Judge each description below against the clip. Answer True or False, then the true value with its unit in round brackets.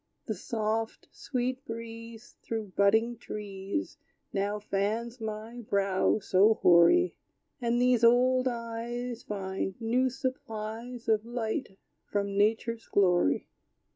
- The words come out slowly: True (105 wpm)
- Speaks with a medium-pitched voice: False (225 Hz)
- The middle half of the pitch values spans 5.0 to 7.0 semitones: False (2.9 semitones)